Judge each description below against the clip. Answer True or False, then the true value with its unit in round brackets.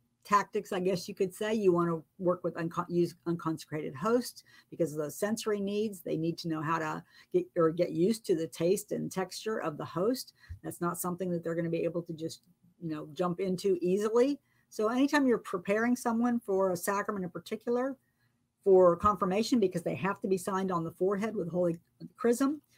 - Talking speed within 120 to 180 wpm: False (205 wpm)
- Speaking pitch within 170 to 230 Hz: True (185 Hz)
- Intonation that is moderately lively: True (3.8 semitones)